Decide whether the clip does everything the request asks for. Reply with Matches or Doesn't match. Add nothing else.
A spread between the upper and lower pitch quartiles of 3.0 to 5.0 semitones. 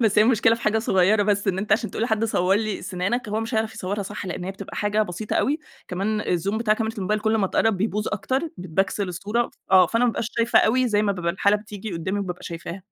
Doesn't match